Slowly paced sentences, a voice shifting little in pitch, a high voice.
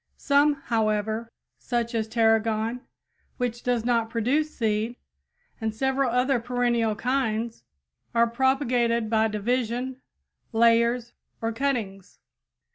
Yes: slow, 105 wpm; narrow, 1.9 semitones; high, 235 Hz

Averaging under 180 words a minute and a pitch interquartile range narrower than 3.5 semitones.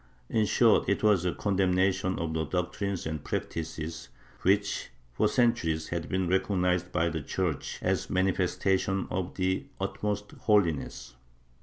Yes: average, 140 wpm; average, 2.8 semitones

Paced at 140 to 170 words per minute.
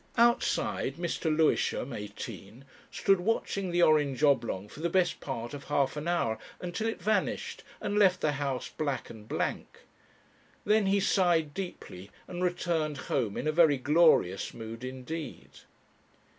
Yes: average, 145 wpm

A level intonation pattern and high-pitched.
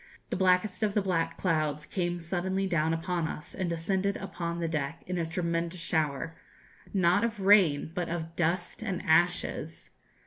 No: narrow, 2.3 semitones; medium, 175 Hz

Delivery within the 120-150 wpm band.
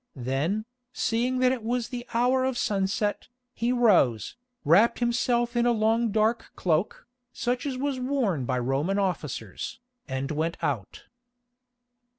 Yes: average, 140 wpm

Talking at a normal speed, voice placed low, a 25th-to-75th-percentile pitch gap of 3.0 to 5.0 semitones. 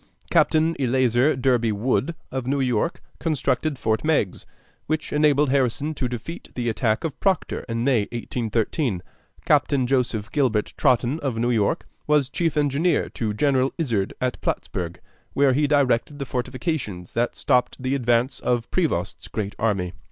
Yes: average, 150 wpm; low, 130 Hz; average, 3.9 semitones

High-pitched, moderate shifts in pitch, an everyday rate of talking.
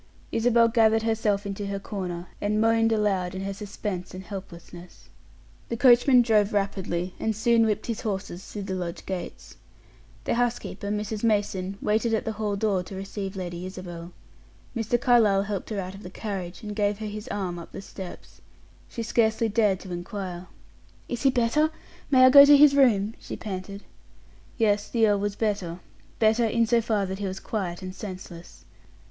Yes: high, 205 Hz; average, 3.0 semitones; average, 180 wpm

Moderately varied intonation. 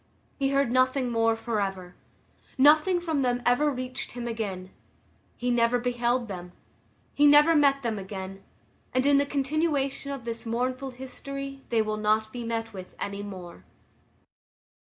Yes: average, 4.1 semitones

